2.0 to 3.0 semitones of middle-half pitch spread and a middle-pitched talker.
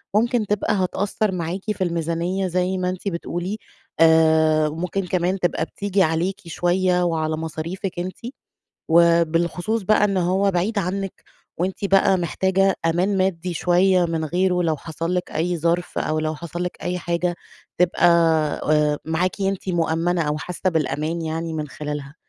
Yes: narrow, 2.5 semitones; medium, 175 Hz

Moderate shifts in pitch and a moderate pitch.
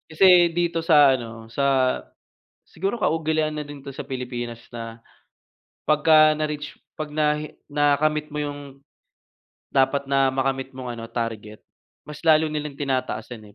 Yes: average, 3.2 semitones; medium, 145 Hz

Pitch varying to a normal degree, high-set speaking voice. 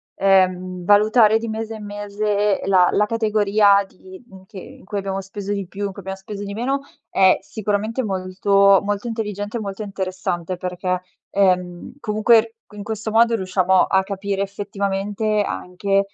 No: narrow, 1.9 semitones; high, 200 Hz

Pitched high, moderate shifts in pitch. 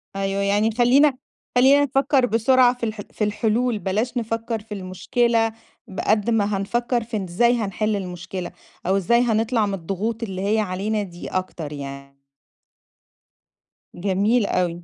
Yes: high, 215 Hz; average, 3.6 semitones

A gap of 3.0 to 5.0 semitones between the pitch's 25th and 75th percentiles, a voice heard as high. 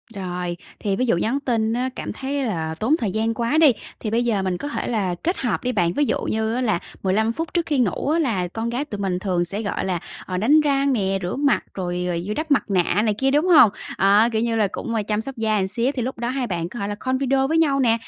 No: wide, 5.5 semitones; high, 225 Hz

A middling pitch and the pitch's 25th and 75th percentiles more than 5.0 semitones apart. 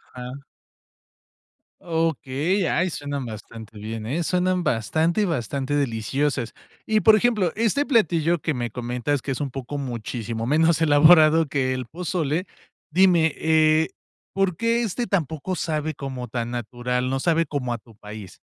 Yes: medium, 145 Hz; wide, 5.5 semitones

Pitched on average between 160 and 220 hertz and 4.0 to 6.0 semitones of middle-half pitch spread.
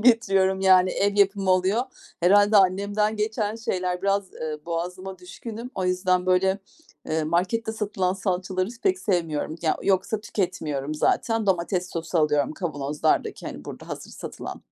No: medium, 185 Hz; narrow, 2.4 semitones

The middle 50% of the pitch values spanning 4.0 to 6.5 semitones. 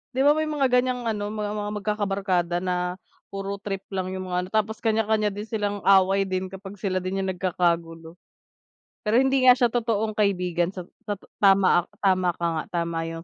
No: average, 2.7 semitones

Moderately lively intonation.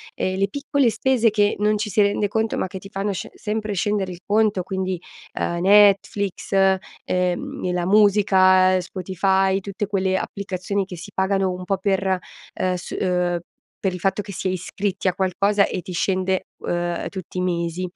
No: narrow, 1.9 semitones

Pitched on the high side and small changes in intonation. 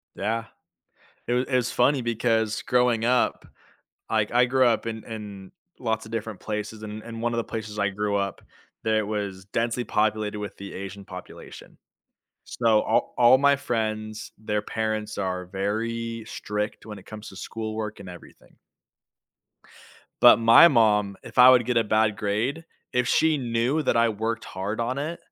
No: low, 110 Hz; narrow, 2.1 semitones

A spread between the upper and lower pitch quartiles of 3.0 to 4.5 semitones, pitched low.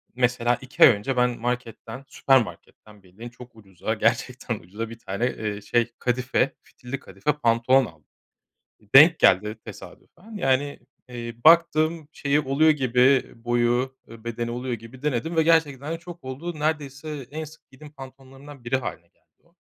Yes: average, 3.7 semitones; low, 130 Hz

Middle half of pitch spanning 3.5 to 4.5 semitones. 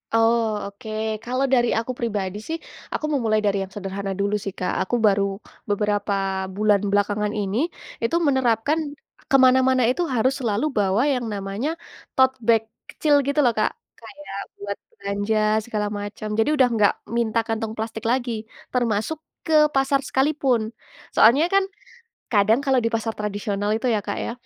Yes: average, 4.0 semitones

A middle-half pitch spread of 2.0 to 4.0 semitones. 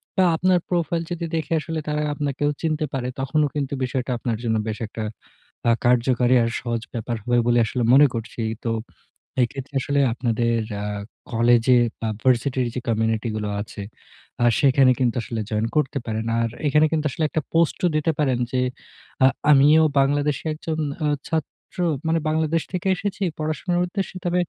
No: average, 4.8 semitones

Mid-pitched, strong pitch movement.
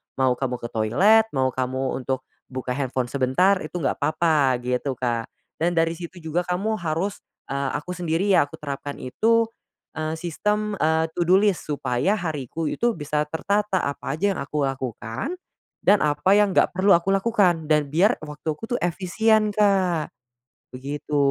Yes: medium, 160 Hz; wide, 6.0 semitones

